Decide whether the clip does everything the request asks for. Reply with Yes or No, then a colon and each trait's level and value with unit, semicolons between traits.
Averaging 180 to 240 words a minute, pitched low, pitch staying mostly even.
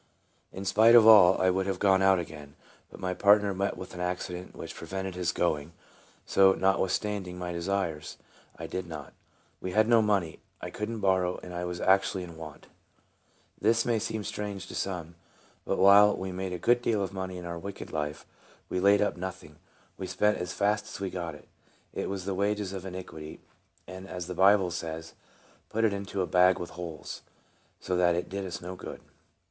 Yes: average, 200 wpm; very low, 95 Hz; narrow, 2.1 semitones